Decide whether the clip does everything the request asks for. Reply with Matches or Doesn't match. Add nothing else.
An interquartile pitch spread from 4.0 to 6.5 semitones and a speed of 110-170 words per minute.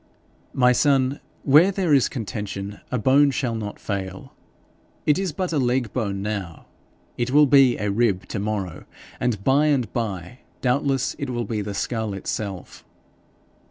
Matches